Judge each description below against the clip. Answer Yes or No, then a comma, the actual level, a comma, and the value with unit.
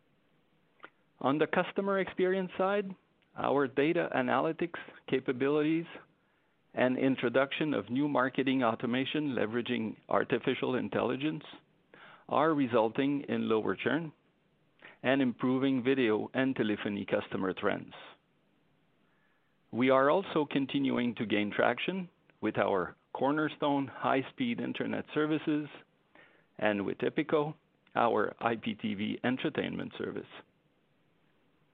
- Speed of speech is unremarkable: No, slow, 95 wpm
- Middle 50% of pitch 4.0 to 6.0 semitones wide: Yes, average, 4.5 semitones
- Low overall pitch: No, medium, 145 Hz